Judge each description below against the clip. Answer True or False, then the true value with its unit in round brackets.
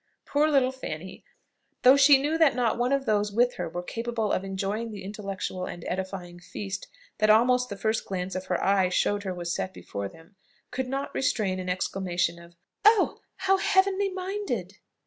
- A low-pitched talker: False (210 Hz)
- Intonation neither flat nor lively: False (6.2 semitones)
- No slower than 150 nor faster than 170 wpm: False (185 wpm)